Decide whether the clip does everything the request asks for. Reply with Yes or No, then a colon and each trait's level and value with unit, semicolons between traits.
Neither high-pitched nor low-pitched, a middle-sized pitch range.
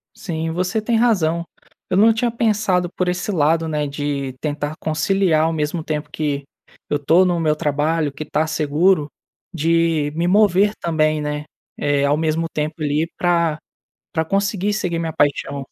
Yes: medium, 160 Hz; average, 3.3 semitones